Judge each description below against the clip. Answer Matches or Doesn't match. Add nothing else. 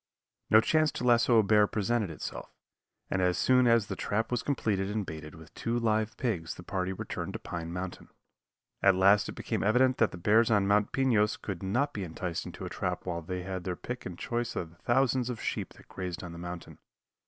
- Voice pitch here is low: Matches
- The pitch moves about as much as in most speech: Matches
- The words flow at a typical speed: Doesn't match